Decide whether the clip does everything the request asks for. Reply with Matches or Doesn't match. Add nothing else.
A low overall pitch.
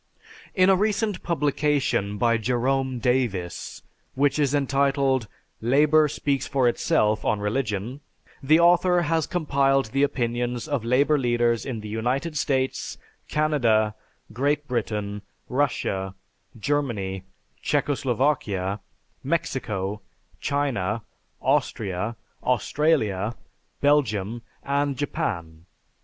Matches